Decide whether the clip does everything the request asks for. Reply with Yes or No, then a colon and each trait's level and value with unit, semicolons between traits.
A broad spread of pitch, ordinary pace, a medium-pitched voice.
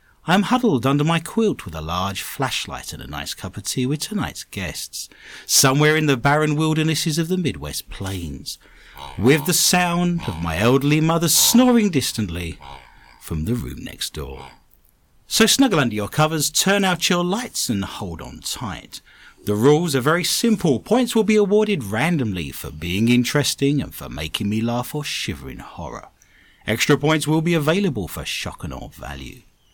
Yes: wide, 8.8 semitones; average, 175 wpm; medium, 150 Hz